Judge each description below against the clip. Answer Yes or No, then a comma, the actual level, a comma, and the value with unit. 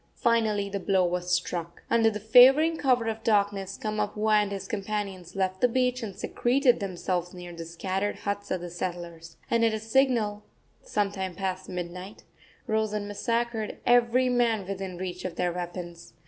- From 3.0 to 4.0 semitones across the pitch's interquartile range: Yes, average, 3.6 semitones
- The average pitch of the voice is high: Yes, high, 200 Hz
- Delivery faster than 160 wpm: Yes, average, 170 wpm